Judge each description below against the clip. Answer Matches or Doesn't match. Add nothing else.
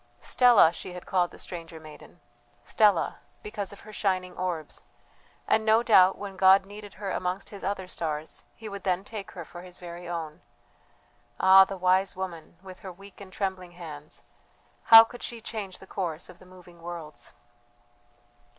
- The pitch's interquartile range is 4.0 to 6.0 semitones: Doesn't match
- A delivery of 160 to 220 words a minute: Matches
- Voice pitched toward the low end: Doesn't match